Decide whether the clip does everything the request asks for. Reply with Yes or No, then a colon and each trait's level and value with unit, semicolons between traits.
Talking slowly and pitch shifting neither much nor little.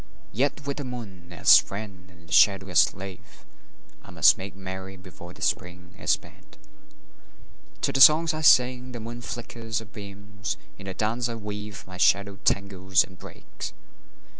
No: average, 165 wpm; average, 3.8 semitones